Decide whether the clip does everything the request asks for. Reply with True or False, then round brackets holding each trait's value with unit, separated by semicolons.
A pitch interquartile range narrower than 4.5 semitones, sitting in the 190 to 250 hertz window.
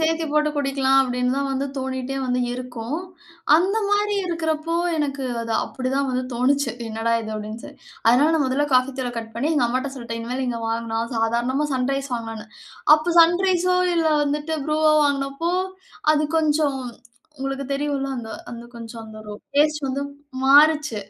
False (3.8 semitones; 275 Hz)